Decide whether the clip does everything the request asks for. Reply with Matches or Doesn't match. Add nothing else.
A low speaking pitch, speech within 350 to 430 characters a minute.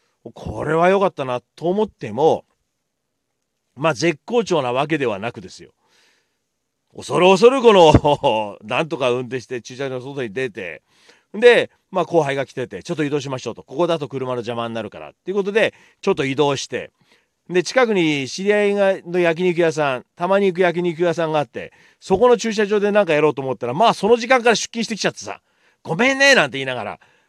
Doesn't match